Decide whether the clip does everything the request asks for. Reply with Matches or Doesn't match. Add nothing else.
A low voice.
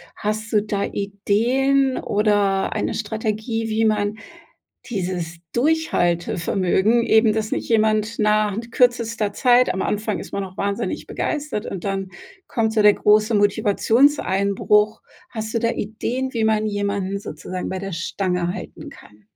Doesn't match